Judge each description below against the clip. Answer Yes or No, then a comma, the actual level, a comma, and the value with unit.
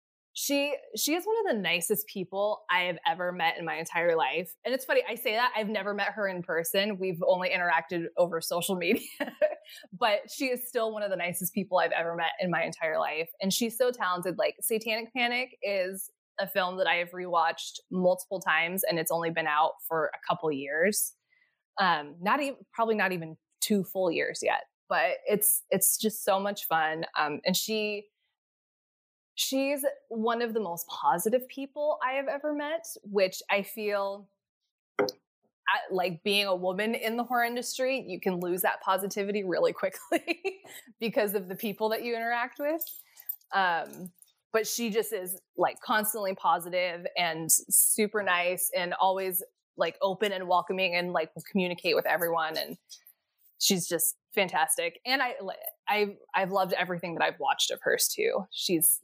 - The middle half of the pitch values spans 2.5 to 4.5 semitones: No, average, 5.1 semitones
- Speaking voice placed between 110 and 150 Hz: No, high, 200 Hz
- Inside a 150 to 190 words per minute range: Yes, average, 175 wpm